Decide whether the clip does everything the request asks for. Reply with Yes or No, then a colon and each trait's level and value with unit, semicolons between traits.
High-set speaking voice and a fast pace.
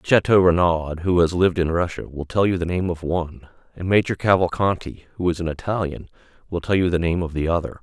No: very low, 85 Hz; fast, 220 wpm